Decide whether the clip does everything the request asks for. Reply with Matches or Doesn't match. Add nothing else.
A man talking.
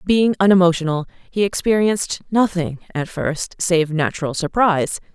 Doesn't match